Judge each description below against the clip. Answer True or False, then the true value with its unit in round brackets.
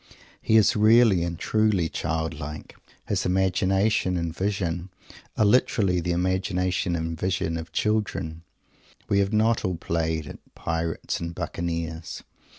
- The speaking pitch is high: False (90 Hz)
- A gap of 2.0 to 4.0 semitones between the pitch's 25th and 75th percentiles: True (3.3 semitones)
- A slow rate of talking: True (130 wpm)